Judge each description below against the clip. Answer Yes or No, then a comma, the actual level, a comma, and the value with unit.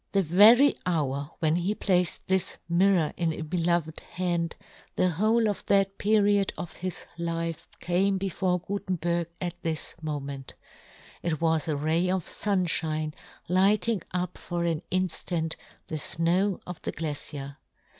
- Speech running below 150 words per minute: Yes, average, 140 wpm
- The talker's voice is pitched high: No, medium, 175 Hz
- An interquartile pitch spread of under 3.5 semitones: Yes, average, 2.9 semitones